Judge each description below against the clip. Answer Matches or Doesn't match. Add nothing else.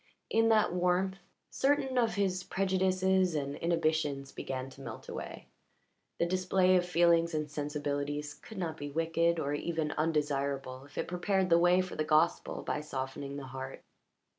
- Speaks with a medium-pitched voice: Matches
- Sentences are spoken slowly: Doesn't match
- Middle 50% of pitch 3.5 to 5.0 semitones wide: Matches